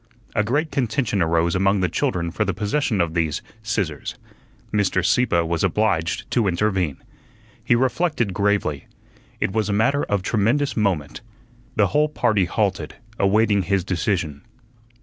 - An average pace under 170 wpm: Yes, average, 145 wpm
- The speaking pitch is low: Yes, low, 100 Hz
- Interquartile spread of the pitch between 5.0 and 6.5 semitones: No, average, 4.3 semitones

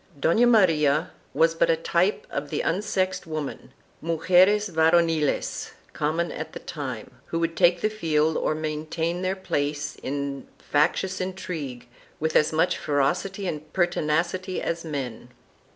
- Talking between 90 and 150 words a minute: Yes, average, 140 wpm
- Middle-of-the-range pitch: Yes, medium, 165 Hz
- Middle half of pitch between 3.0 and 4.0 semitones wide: Yes, average, 3.3 semitones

